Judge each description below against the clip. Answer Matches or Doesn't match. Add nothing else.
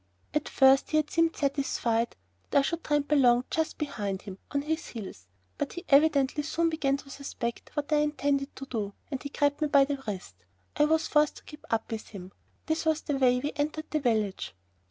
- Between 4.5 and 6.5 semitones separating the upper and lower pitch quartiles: Doesn't match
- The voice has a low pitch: Doesn't match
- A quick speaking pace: Matches